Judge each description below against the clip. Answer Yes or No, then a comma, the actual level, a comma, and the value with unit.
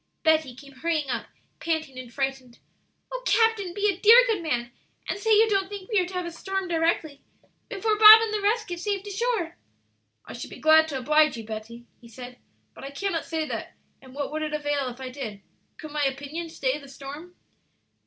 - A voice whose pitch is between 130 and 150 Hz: No, very high, 315 Hz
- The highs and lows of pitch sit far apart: Yes, wide, 6.4 semitones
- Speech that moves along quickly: Yes, fast, 215 wpm